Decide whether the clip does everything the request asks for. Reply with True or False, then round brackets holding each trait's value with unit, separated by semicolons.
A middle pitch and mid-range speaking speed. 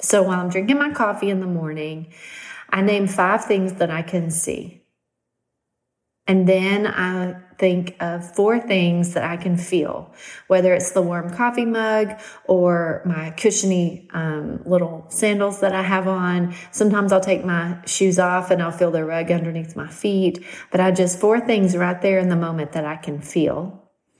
True (180 Hz; 180 wpm)